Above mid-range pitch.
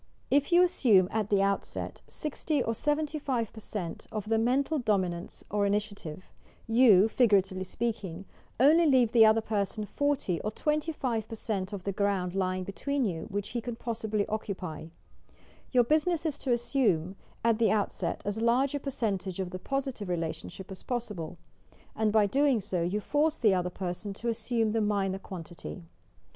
Yes: high, 215 Hz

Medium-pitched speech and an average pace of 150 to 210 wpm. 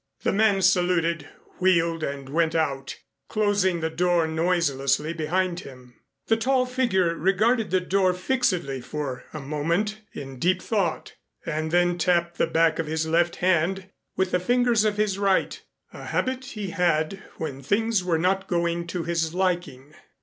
Yes: medium, 175 Hz; average, 155 wpm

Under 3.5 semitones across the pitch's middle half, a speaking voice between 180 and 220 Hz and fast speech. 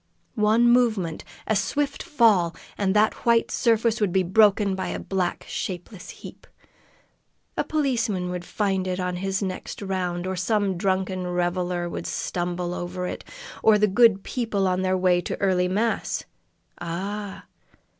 No: average, 2.9 semitones; high, 190 Hz; average, 150 wpm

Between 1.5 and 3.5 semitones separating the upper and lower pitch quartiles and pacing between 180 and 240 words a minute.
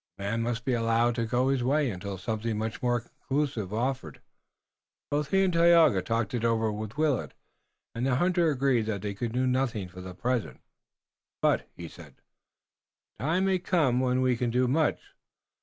No: average, 3.9 semitones; average, 185 wpm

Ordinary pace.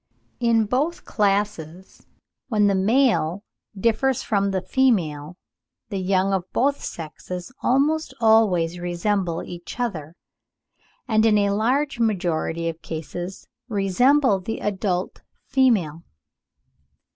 No: slow, 110 wpm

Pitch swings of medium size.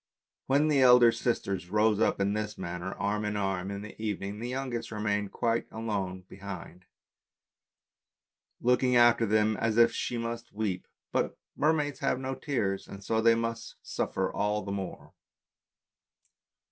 Yes: average, 3.1 semitones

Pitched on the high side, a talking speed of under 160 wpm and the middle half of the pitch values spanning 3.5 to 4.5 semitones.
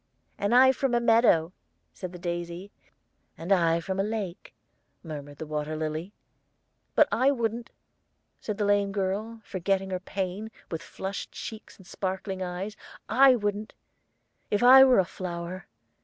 Yes: high, 195 Hz; average, 150 wpm; average, 4.0 semitones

